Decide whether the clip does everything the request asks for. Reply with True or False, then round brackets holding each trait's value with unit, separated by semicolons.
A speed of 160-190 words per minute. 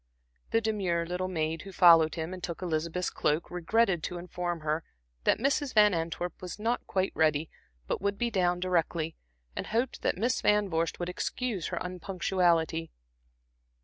True (165 wpm)